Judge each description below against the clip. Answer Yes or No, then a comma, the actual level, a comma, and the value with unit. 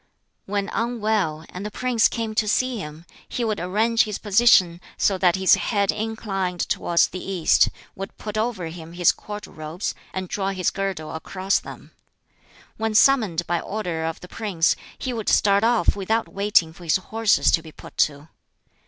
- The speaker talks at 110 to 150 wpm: No, average, 175 wpm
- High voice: Yes, high, 195 Hz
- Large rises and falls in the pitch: No, average, 3.9 semitones